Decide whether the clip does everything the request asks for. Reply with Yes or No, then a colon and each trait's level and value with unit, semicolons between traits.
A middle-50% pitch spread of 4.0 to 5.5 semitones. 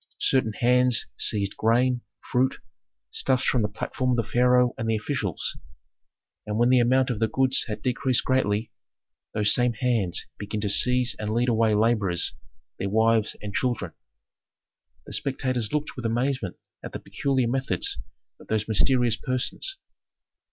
No: average, 2.9 semitones